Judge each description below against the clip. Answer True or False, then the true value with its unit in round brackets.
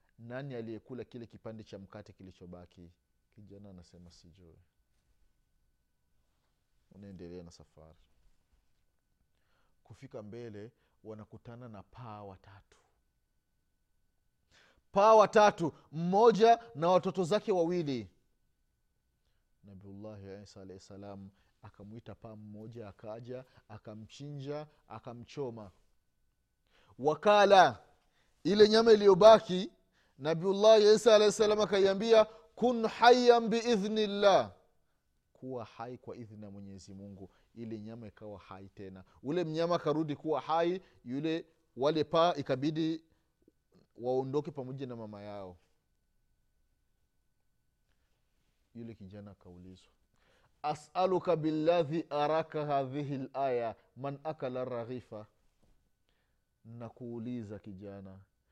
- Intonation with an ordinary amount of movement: False (8.4 semitones)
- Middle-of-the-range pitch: False (115 Hz)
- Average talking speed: False (85 wpm)